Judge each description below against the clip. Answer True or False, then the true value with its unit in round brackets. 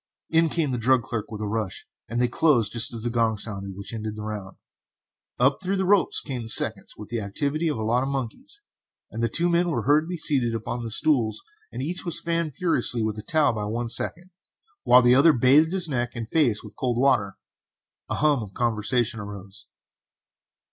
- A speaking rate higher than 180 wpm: True (205 wpm)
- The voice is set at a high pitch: False (120 Hz)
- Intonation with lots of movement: True (5.8 semitones)